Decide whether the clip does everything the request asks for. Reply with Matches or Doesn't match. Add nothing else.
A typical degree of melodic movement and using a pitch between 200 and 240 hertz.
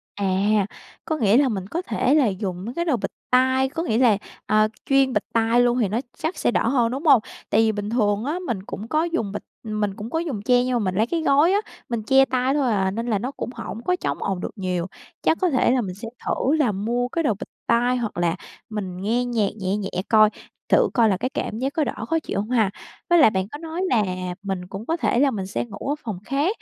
Matches